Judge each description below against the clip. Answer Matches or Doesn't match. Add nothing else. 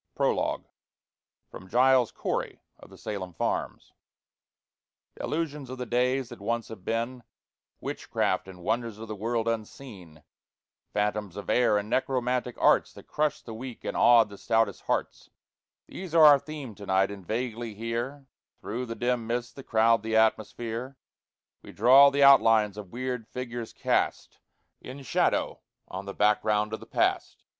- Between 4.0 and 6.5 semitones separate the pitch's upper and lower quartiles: Doesn't match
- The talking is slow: Doesn't match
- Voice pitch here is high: Doesn't match